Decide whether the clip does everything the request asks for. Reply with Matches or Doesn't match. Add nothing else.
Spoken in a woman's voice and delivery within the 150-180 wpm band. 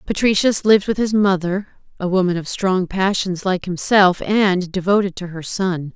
Matches